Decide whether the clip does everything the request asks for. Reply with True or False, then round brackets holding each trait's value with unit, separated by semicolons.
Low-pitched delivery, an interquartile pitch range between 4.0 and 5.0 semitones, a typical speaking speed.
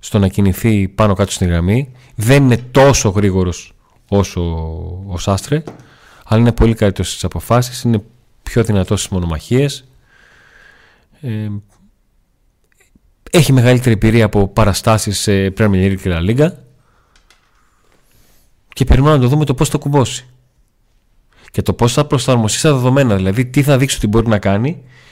True (110 Hz; 4.7 semitones; 140 wpm)